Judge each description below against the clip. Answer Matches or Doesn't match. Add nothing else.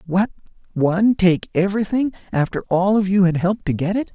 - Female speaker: Doesn't match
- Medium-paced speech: Matches